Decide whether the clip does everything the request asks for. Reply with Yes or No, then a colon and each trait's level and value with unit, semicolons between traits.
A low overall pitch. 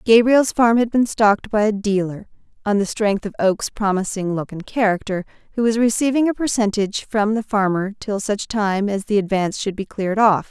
No: high, 210 Hz